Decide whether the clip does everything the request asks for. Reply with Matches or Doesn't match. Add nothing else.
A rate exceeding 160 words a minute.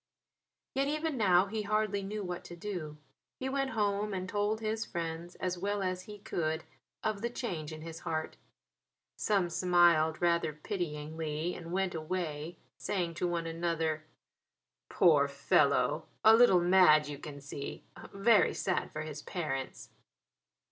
Doesn't match